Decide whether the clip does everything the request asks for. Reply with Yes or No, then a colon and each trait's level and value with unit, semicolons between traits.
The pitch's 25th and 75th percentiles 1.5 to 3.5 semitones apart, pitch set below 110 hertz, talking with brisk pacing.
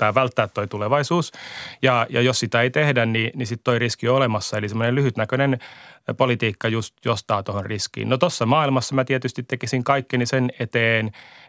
No: narrow, 2.6 semitones; low, 120 Hz; fast, 185 wpm